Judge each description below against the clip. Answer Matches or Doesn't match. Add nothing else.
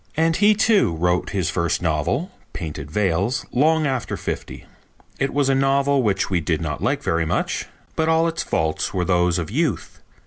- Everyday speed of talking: Matches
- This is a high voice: Doesn't match